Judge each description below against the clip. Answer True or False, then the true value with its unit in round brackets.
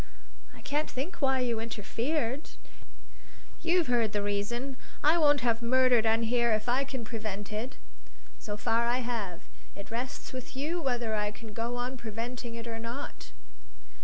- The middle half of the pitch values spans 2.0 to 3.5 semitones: True (2.6 semitones)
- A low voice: False (235 Hz)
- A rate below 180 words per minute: True (160 wpm)